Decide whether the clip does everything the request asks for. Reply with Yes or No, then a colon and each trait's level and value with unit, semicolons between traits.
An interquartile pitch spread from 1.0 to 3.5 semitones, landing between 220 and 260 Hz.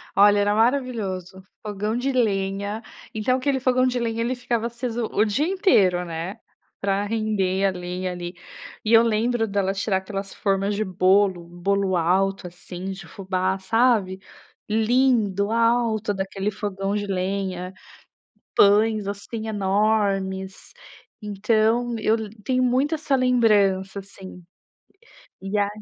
No: average, 3.1 semitones; high, 205 Hz